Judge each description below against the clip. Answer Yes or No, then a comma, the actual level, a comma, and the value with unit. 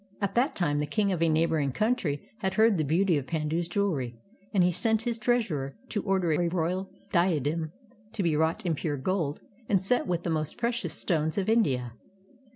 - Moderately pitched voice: Yes, medium, 170 Hz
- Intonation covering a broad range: No, average, 4.5 semitones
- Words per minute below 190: No, average, 200 wpm